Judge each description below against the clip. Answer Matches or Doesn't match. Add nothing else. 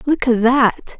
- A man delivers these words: Doesn't match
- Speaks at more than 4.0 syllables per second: Doesn't match